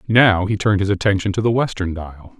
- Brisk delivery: Yes, fast, 225 wpm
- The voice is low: Yes, low, 100 Hz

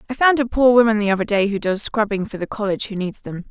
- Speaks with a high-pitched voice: Yes, high, 210 Hz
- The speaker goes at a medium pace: No, fast, 290 wpm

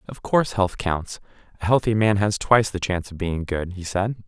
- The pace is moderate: No, fast, 210 wpm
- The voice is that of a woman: No, male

